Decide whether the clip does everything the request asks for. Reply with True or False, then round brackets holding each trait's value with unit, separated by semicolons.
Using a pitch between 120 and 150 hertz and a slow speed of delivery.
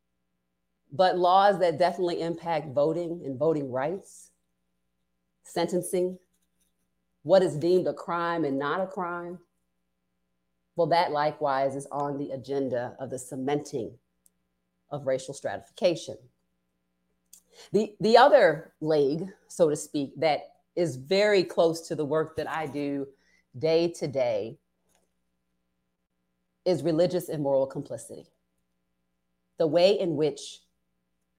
True (140 Hz; 115 wpm)